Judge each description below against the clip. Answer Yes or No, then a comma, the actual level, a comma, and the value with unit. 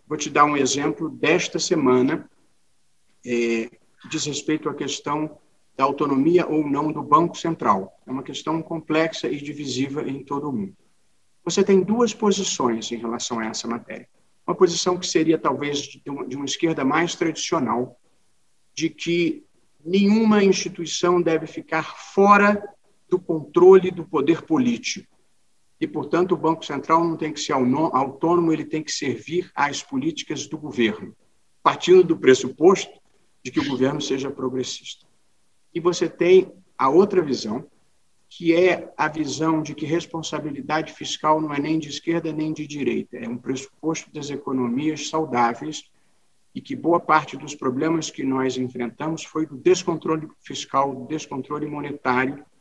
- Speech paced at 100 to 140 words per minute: No, average, 150 wpm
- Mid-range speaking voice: Yes, medium, 155 Hz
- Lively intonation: No, average, 3.7 semitones